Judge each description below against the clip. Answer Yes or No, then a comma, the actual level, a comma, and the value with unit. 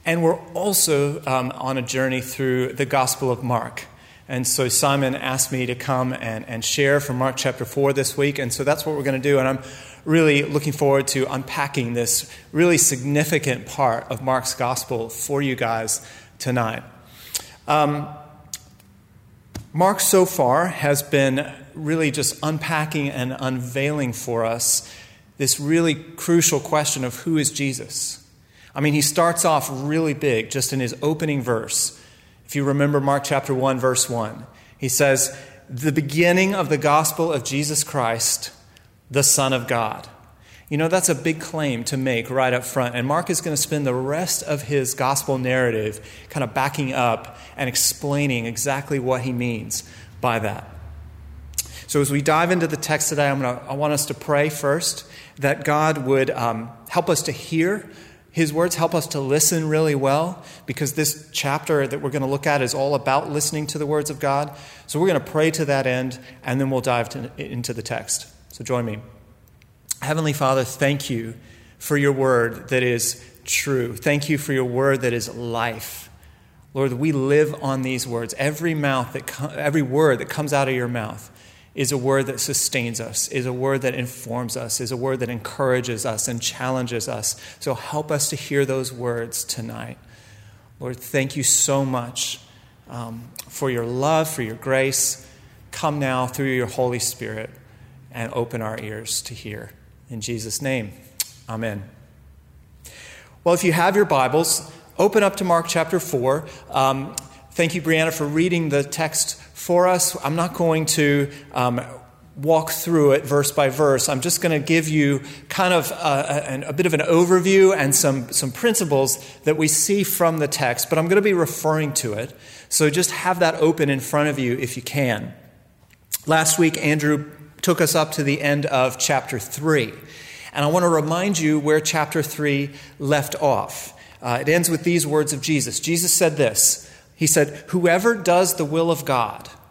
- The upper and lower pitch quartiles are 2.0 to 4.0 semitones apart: Yes, average, 3.7 semitones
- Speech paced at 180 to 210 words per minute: Yes, average, 185 wpm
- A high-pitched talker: No, medium, 140 Hz